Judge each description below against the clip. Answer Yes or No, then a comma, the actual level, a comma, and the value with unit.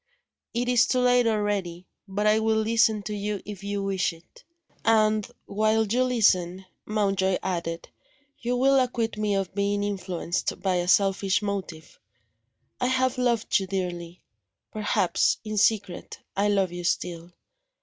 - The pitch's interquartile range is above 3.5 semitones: No, average, 2.9 semitones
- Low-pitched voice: No, high, 205 Hz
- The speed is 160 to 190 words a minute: No, average, 150 wpm